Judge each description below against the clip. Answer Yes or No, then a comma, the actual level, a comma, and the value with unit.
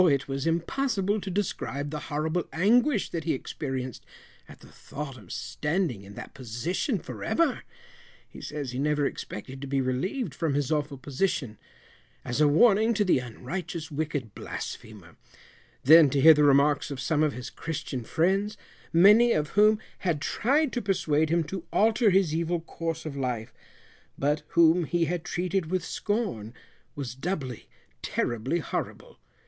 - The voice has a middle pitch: Yes, medium, 155 Hz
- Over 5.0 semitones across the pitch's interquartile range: Yes, wide, 5.4 semitones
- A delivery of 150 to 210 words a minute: Yes, average, 160 wpm